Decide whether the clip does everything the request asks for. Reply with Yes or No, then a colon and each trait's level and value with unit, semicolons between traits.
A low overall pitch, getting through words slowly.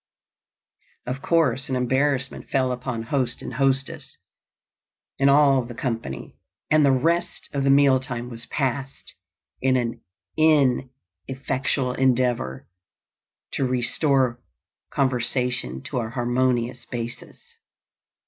Yes: low, 130 Hz; slow, 110 wpm